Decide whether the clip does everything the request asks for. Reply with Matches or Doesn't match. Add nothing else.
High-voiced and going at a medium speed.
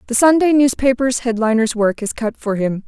Matches